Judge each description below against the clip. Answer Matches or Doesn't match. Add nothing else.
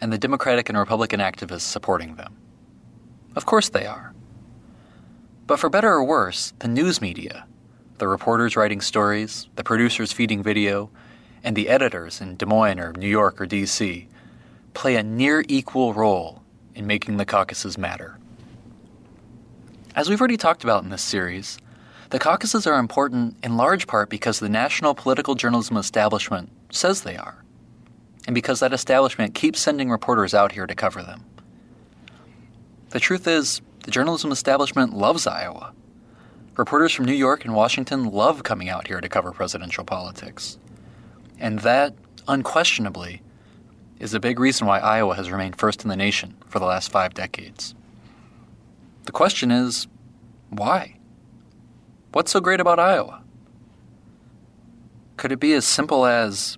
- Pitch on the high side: Doesn't match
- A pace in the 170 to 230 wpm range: Doesn't match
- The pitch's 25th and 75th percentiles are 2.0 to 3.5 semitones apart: Doesn't match